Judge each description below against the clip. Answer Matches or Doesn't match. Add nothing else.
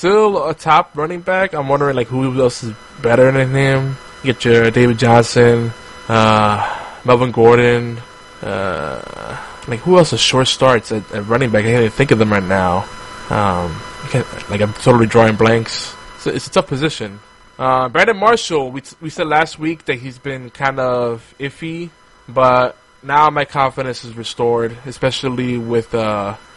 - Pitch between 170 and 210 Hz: Doesn't match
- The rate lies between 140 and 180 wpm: Matches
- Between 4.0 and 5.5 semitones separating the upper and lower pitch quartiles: Doesn't match